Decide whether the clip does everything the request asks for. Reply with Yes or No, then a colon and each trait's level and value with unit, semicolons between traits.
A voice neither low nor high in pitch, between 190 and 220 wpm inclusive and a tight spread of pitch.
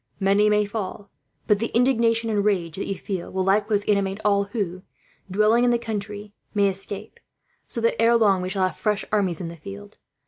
No: high, 205 Hz; average, 200 wpm; narrow, 1.9 semitones